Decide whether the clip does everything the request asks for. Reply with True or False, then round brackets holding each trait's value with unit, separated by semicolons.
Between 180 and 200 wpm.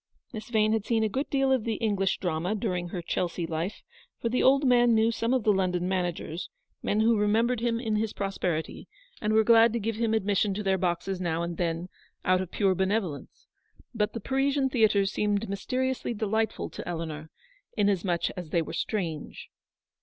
True (190 wpm)